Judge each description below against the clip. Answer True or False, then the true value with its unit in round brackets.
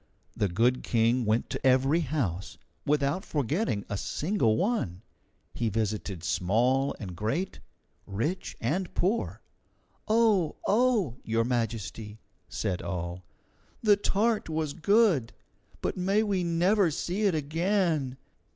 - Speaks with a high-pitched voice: False (140 Hz)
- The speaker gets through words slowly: True (120 wpm)